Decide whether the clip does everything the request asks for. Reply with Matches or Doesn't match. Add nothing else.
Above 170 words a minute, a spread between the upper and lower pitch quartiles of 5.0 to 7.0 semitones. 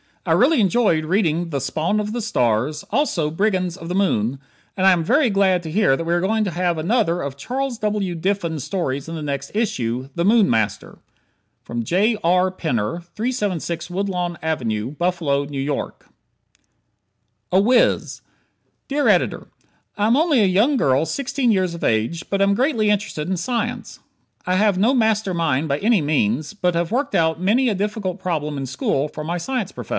Matches